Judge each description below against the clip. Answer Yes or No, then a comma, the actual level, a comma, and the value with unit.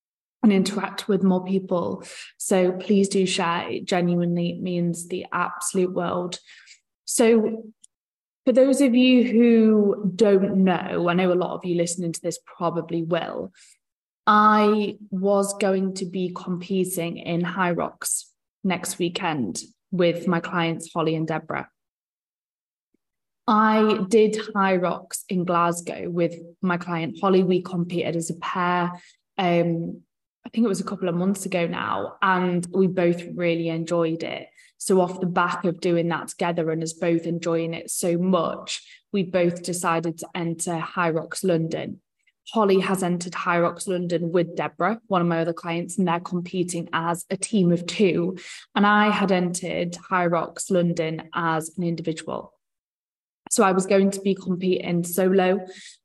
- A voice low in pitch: No, medium, 180 Hz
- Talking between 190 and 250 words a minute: No, average, 155 wpm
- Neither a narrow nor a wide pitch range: No, narrow, 2.3 semitones